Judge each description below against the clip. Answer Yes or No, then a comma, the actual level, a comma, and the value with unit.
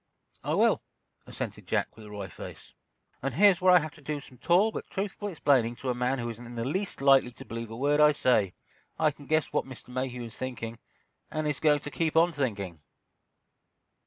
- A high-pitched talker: No, low, 135 Hz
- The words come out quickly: Yes, fast, 215 wpm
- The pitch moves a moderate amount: Yes, average, 4.7 semitones